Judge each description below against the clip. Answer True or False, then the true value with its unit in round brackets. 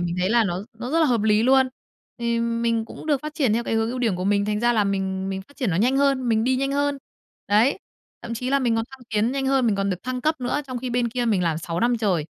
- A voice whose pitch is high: True (235 Hz)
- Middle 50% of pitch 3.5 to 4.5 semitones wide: True (4.0 semitones)